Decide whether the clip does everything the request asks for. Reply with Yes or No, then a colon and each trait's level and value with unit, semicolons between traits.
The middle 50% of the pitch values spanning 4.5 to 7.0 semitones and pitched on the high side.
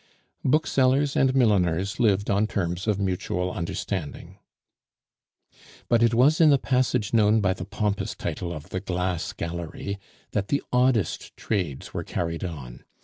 No: average, 5.0 semitones; low, 100 Hz